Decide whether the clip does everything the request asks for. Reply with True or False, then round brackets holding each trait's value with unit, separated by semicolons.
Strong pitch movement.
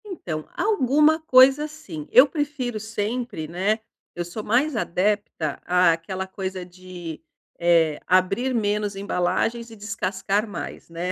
True (5.8 semitones)